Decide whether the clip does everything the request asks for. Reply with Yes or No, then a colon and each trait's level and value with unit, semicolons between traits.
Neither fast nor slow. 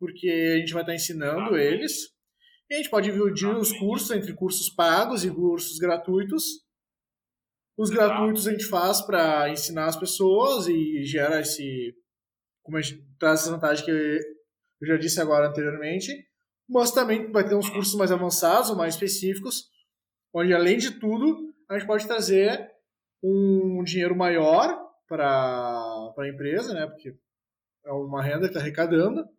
Yes: average, 155 wpm